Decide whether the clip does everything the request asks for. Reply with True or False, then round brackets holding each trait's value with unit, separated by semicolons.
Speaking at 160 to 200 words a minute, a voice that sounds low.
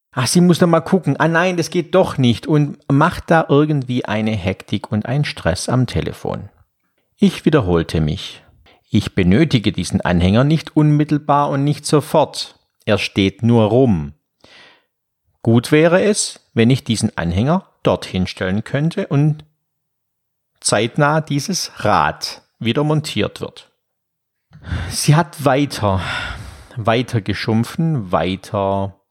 False (130 wpm; 130 Hz)